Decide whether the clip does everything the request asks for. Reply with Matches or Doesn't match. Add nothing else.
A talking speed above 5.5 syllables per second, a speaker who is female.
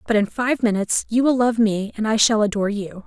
Matches